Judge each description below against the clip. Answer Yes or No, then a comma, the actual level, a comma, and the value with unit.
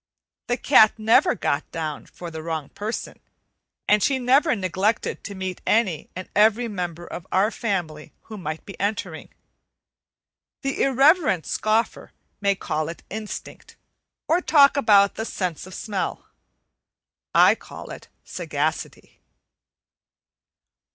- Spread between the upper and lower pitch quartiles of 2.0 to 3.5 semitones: No, average, 4.6 semitones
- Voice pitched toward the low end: No, high, 200 Hz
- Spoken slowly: Yes, slow, 125 wpm